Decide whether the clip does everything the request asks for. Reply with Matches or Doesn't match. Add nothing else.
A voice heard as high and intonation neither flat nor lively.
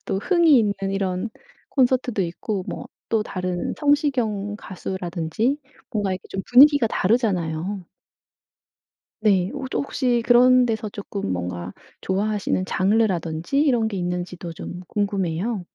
Matches